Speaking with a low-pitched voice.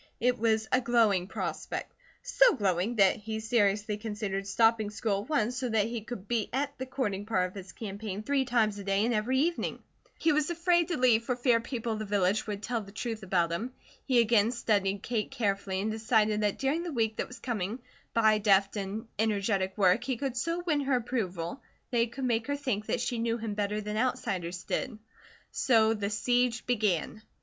No: high, 220 Hz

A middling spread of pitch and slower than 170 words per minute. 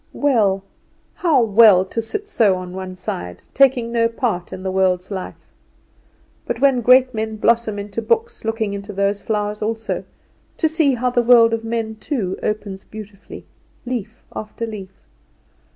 Yes: average, 3.2 semitones; average, 155 wpm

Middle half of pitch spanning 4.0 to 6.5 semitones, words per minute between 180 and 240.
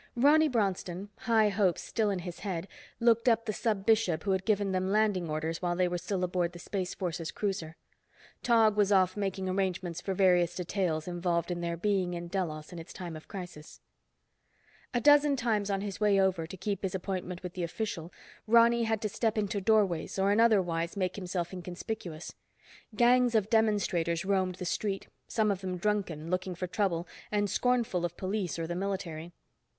No: average, 3.2 semitones; average, 190 wpm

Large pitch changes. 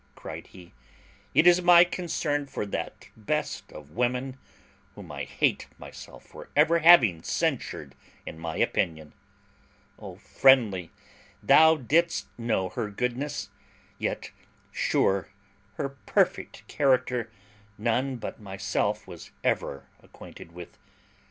Yes: wide, 7.2 semitones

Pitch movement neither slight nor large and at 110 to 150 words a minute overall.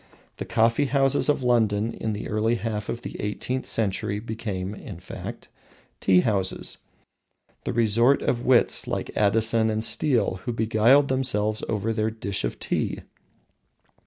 No: narrow, 2.3 semitones; average, 145 wpm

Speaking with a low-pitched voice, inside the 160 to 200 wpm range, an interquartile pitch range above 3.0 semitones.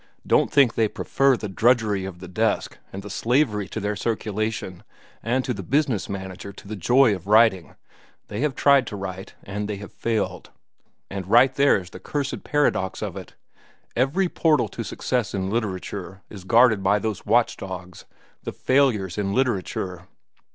Yes: low, 105 Hz; average, 170 wpm; average, 4.3 semitones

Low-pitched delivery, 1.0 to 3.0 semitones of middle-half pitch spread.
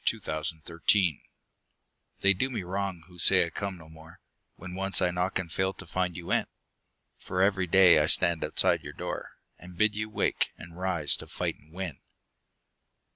Yes: very low, 90 Hz; narrow, 2.4 semitones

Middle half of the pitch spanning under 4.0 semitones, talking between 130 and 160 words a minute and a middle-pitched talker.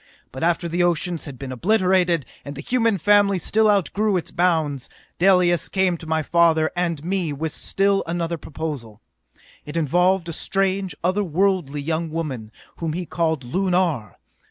Yes: average, 3.2 semitones; average, 155 wpm; medium, 170 Hz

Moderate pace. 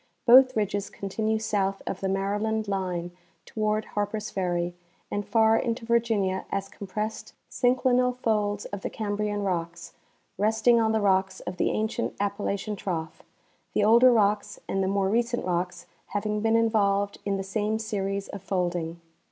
Yes: average, 155 wpm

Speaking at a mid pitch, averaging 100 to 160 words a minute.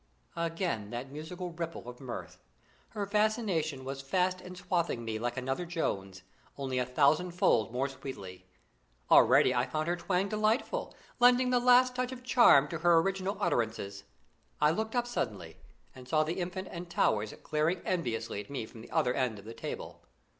No: medium, 155 Hz; average, 170 wpm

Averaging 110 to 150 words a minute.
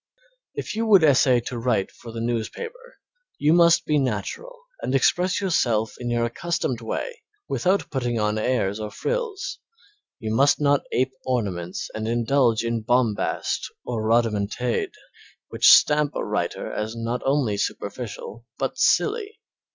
Yes: average, 145 wpm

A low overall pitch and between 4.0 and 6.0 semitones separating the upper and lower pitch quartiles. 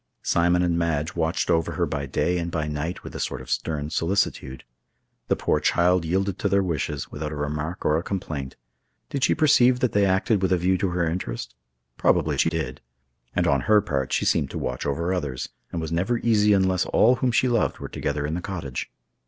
Yes: very low, 85 Hz; average, 4.3 semitones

